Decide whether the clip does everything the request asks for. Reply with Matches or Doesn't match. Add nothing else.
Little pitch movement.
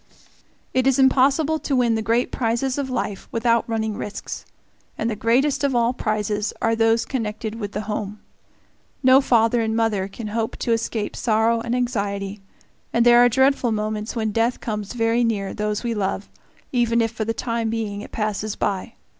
Matches